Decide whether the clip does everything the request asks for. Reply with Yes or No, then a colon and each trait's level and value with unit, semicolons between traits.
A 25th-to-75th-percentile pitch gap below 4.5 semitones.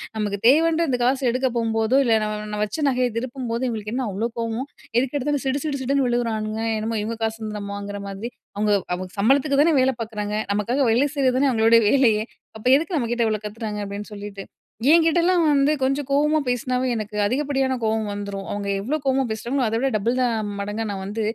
Yes: average, 4.1 semitones